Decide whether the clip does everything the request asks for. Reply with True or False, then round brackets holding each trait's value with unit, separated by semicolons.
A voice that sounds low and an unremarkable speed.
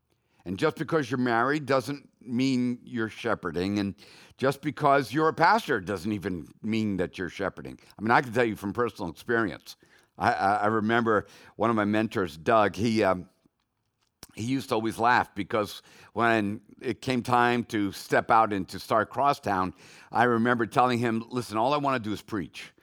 True (115 Hz; 180 wpm)